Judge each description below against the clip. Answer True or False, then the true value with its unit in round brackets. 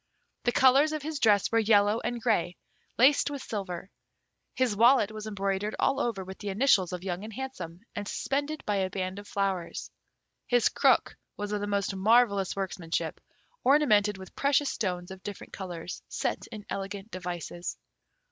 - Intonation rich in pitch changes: False (4.1 semitones)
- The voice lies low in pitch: False (205 Hz)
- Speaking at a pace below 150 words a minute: False (165 wpm)